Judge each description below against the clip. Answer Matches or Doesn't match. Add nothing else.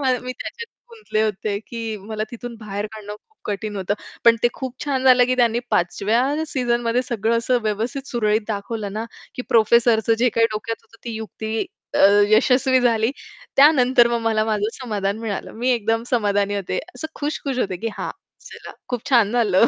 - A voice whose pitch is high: Matches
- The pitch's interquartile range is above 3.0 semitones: Doesn't match